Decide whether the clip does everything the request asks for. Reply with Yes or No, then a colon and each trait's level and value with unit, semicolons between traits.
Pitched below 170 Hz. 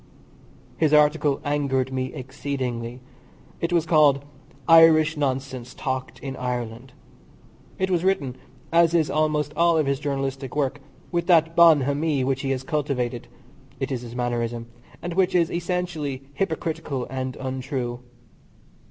Yes: medium, 140 Hz